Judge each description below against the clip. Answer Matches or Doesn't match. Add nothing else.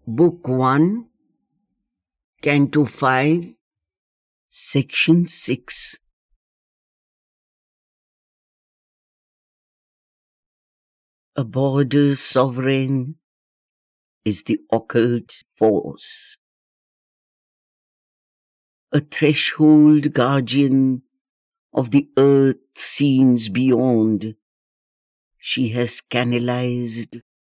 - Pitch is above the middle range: Doesn't match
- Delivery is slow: Matches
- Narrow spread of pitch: Doesn't match